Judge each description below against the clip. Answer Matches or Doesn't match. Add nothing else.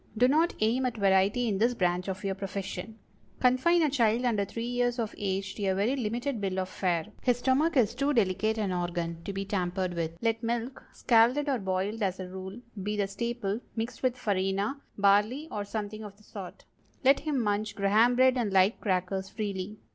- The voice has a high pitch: Matches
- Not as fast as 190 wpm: Doesn't match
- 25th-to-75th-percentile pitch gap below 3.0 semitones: Doesn't match